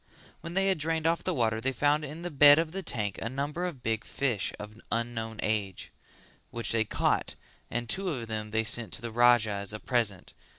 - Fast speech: Yes, fast, 215 wpm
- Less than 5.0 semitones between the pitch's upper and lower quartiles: No, average, 5.3 semitones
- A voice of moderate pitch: No, low, 120 Hz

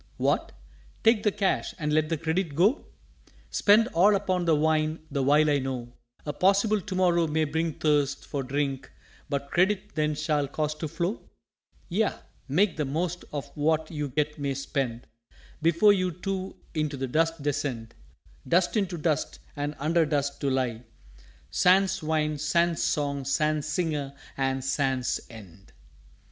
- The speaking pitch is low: No, medium, 155 Hz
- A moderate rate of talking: Yes, average, 155 wpm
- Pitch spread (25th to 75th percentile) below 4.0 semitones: Yes, average, 3.6 semitones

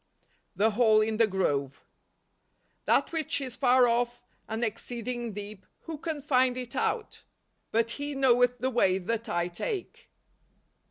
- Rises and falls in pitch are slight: No, average, 3.2 semitones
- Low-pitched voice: No, high, 240 Hz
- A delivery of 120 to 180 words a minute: Yes, average, 160 wpm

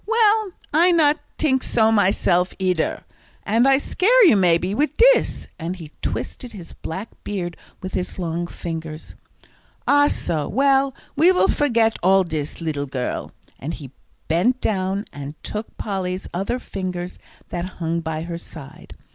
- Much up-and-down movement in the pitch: Yes, wide, 7.8 semitones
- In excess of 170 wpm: No, average, 150 wpm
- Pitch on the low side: No, high, 190 Hz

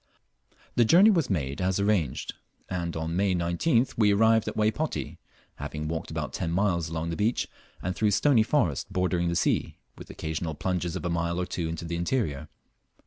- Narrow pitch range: No, average, 4.4 semitones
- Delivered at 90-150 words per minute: No, average, 185 wpm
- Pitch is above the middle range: No, very low, 90 Hz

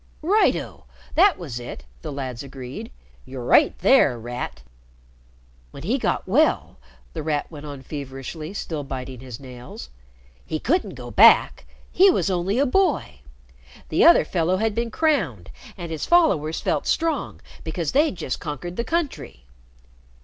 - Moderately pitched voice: Yes, medium, 155 Hz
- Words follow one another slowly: No, average, 150 wpm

